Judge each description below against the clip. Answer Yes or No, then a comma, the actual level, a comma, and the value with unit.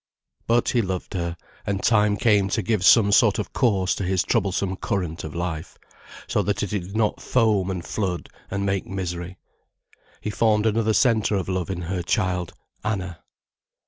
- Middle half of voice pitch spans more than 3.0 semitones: No, average, 2.7 semitones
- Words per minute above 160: Yes, average, 175 wpm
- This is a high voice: No, very low, 95 Hz